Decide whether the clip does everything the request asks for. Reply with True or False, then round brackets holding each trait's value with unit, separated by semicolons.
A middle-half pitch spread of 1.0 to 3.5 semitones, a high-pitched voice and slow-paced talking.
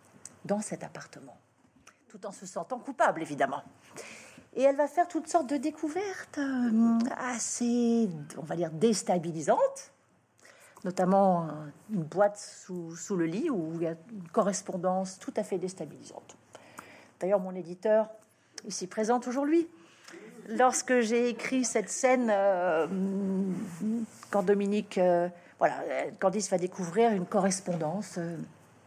False (4.7 semitones; 205 Hz; 125 wpm)